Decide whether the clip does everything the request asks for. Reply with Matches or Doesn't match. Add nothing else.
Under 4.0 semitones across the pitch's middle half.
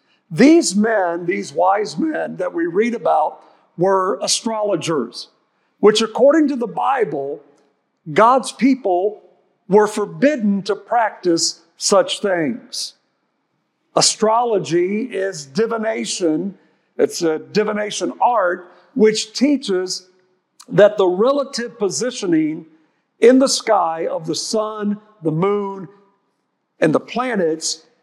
Doesn't match